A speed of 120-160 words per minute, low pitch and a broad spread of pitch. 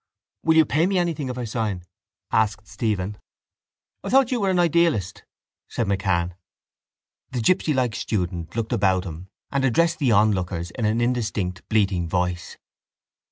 Yes: average, 150 wpm; low, 110 Hz; wide, 7.3 semitones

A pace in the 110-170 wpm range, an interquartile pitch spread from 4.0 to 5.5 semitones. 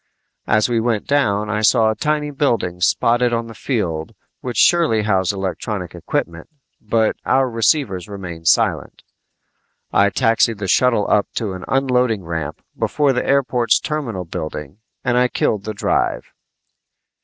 Yes: average, 145 wpm; average, 4.6 semitones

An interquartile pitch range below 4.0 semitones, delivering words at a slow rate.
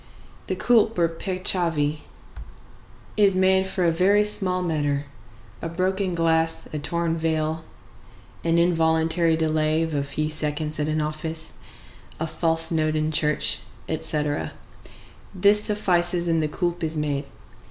Yes: narrow, 2.4 semitones; slow, 130 wpm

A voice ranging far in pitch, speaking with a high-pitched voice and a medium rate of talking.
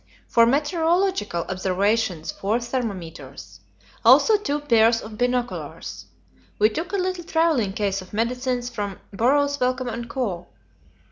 No: wide, 6.1 semitones; high, 235 Hz; slow, 125 wpm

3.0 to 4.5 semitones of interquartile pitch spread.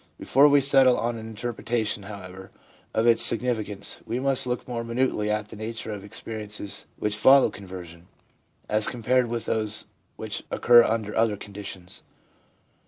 No: narrow, 2.6 semitones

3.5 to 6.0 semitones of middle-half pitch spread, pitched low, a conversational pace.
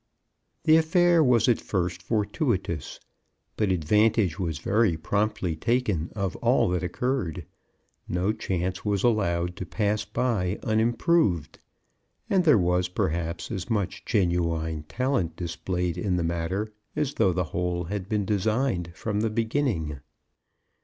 No: average, 4.3 semitones; very low, 95 Hz; slow, 130 wpm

